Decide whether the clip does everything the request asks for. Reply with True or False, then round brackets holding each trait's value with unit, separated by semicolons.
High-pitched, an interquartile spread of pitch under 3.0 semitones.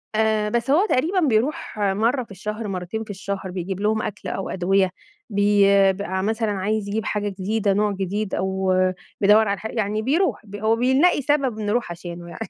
True (210 Hz; 2.5 semitones)